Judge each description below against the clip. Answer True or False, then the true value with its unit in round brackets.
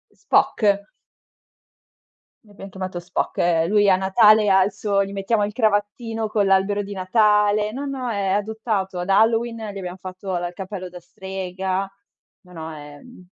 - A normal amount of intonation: False (2.3 semitones)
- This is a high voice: True (195 Hz)